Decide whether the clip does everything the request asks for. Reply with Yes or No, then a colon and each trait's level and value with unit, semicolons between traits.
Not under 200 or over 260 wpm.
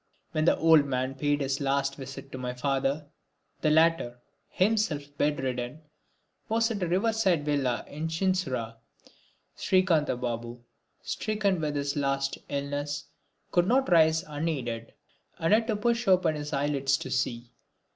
No: average, 145 wpm